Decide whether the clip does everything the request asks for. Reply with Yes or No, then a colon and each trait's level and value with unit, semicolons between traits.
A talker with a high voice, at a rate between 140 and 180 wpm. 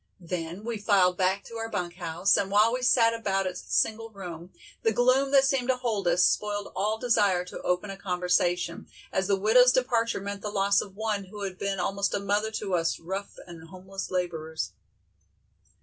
No: high, 200 Hz; average, 195 wpm